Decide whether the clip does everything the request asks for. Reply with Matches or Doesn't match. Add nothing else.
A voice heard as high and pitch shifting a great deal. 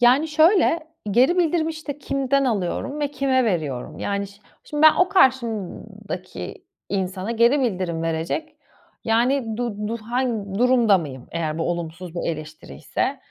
Matches